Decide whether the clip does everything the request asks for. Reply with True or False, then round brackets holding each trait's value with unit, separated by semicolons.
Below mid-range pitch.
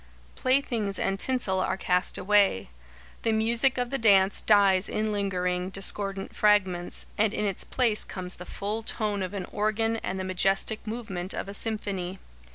False (200 Hz)